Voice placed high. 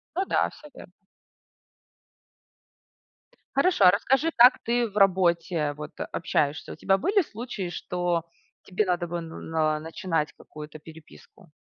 No: medium, 180 Hz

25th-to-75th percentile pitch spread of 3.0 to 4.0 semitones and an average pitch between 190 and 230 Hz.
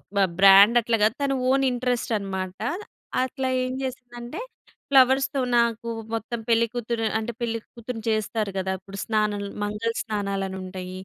Yes: average, 3.4 semitones; high, 225 Hz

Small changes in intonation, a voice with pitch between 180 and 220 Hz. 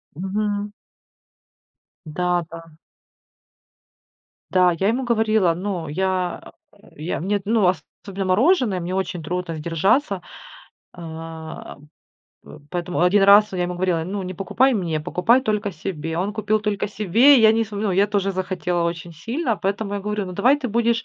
No: average, 3.2 semitones; high, 190 Hz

